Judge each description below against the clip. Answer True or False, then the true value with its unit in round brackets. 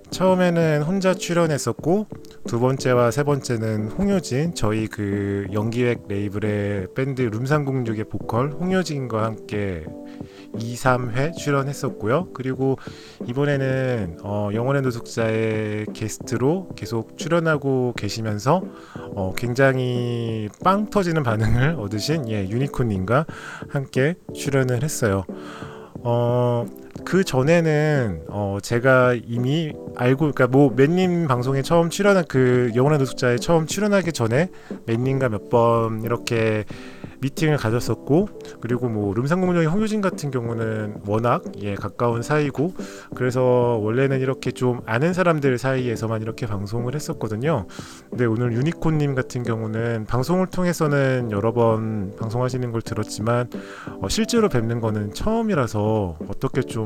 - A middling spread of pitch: True (4.9 semitones)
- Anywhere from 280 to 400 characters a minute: True (295 characters per minute)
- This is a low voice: True (125 Hz)